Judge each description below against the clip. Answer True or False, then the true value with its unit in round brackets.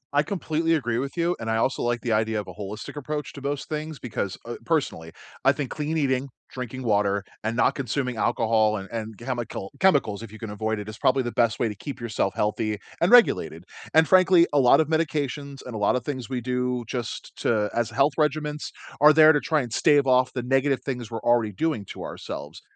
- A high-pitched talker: False (125 Hz)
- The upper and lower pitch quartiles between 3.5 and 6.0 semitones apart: True (4.8 semitones)